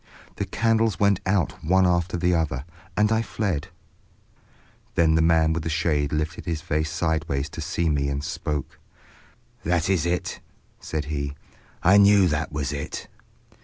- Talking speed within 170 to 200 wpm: No, average, 155 wpm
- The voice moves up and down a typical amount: Yes, average, 3.0 semitones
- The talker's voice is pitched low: Yes, very low, 80 Hz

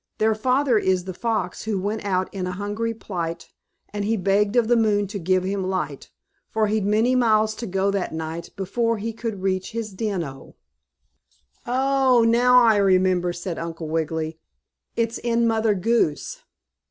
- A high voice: Yes, high, 205 Hz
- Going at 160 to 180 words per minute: Yes, average, 170 wpm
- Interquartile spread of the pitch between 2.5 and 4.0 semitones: Yes, average, 3.7 semitones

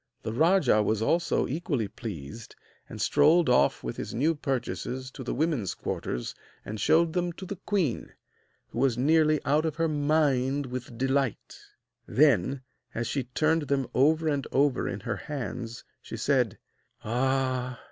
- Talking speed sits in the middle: Yes, average, 155 wpm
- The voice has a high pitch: No, low, 135 Hz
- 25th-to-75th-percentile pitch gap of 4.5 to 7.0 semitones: No, average, 4.1 semitones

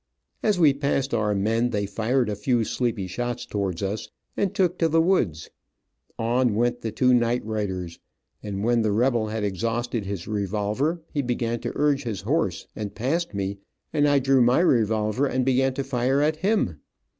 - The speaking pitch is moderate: No, low, 120 Hz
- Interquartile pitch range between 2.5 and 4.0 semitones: No, average, 4.5 semitones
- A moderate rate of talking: Yes, average, 180 wpm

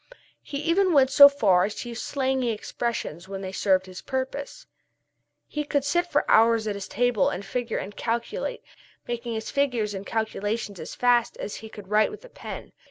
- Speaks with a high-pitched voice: Yes, high, 235 Hz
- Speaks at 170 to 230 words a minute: Yes, average, 190 wpm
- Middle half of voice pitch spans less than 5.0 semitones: No, average, 5.3 semitones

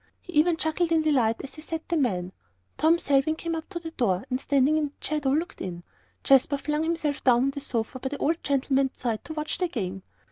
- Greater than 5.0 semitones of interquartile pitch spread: No, average, 3.6 semitones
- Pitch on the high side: Yes, very high, 285 Hz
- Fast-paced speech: Yes, fast, 235 wpm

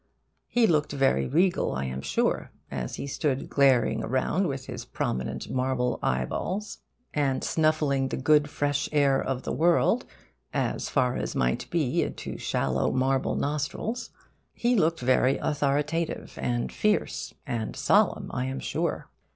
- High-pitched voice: No, low, 135 Hz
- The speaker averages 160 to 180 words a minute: No, average, 145 wpm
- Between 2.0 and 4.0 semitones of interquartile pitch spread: Yes, average, 3.6 semitones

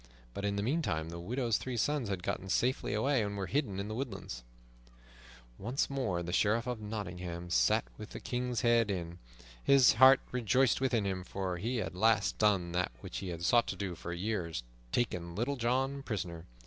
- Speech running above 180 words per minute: Yes, average, 195 wpm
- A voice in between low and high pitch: No, low, 105 Hz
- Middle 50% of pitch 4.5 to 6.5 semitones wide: Yes, wide, 5.6 semitones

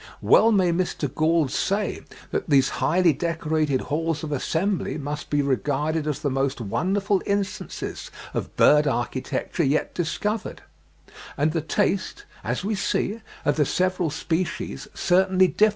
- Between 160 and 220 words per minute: No, average, 140 wpm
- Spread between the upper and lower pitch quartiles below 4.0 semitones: No, average, 4.3 semitones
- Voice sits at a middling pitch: Yes, medium, 160 Hz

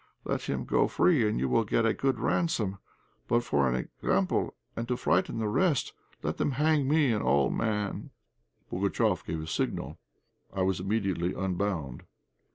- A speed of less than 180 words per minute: Yes, average, 165 wpm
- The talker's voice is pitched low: Yes, low, 105 Hz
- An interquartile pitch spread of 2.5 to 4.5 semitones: No, average, 5.3 semitones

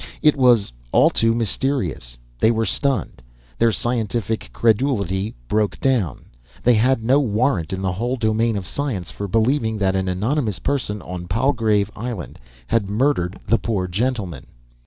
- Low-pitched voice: Yes, low, 110 Hz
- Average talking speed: Yes, average, 150 wpm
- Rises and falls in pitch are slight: No, average, 4.3 semitones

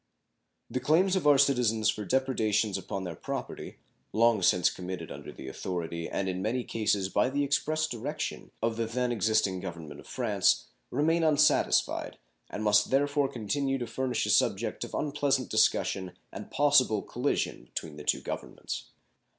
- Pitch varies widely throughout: Yes, wide, 6.5 semitones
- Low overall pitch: Yes, low, 115 Hz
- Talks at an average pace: Yes, average, 160 wpm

